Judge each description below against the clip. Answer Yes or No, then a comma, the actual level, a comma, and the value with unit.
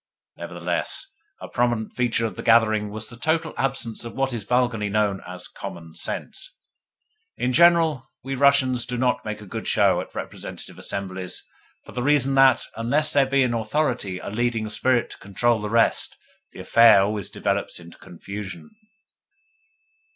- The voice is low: Yes, low, 120 Hz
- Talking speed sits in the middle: Yes, average, 160 wpm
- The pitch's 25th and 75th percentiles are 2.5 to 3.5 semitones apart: No, average, 4.1 semitones